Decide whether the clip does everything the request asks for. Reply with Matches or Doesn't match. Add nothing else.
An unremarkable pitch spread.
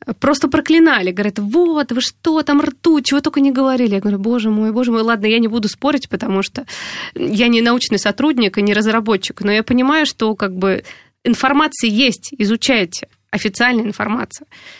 Matches